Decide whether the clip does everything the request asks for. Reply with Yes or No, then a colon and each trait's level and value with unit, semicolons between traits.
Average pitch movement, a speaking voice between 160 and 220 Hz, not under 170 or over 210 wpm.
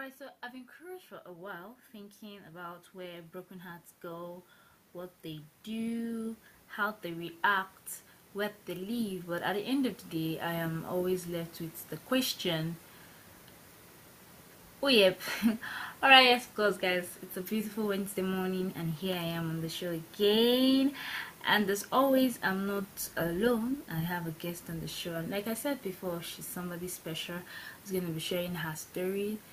Yes: average, 3.9 semitones; medium, 185 Hz; average, 175 wpm